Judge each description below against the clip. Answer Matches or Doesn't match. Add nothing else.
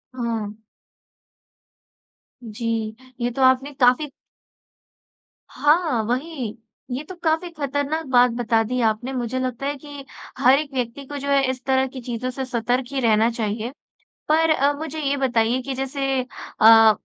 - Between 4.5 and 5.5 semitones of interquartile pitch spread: Doesn't match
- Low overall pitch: Doesn't match